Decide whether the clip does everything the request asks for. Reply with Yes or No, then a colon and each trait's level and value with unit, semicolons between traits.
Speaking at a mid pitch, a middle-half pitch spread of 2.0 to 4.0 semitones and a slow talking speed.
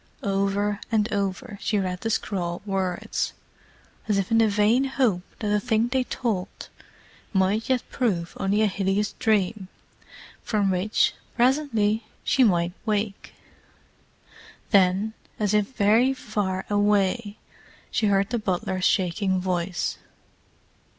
No: high, 205 Hz; narrow, 2.5 semitones; slow, 125 wpm